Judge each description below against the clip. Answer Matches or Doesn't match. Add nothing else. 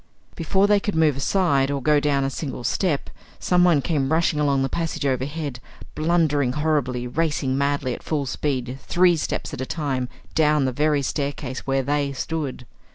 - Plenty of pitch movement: Doesn't match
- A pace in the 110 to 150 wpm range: Doesn't match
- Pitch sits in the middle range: Matches